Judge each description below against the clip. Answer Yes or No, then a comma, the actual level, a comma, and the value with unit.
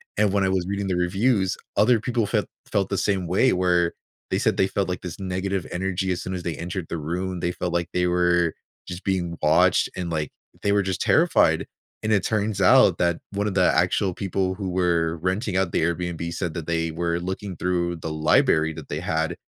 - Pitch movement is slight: Yes, narrow, 2.1 semitones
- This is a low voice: Yes, very low, 90 Hz